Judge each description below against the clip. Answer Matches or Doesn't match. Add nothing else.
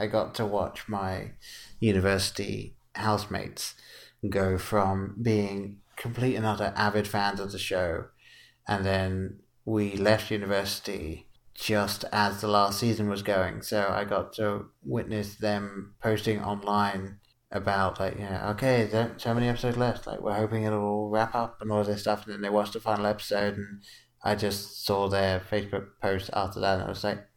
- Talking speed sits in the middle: Matches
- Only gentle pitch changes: Matches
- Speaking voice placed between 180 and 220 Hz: Doesn't match